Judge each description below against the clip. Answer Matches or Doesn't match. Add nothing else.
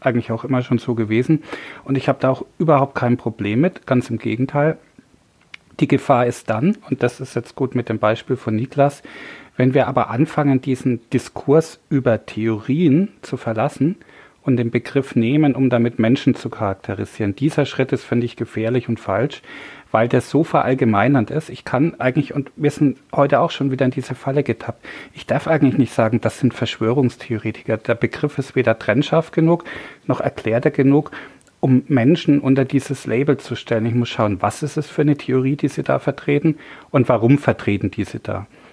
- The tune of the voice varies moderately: Matches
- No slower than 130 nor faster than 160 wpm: Doesn't match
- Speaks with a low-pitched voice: Matches